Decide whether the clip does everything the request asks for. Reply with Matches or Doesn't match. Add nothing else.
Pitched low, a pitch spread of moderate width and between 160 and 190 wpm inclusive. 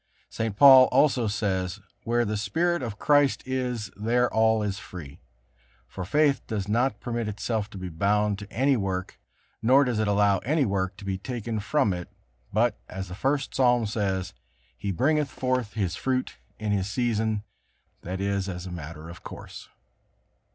Matches